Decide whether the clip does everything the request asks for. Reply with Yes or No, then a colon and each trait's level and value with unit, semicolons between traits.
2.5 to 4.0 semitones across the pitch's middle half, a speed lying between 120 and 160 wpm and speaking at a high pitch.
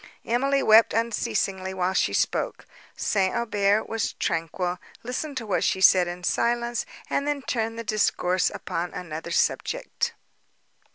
No: average, 4.4 semitones; slow, 135 wpm; high, 210 Hz